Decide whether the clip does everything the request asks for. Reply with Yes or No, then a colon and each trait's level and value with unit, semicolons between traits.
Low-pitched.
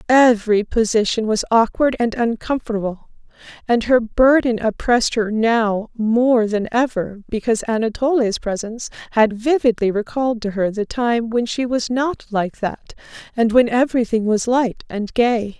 No: high, 230 Hz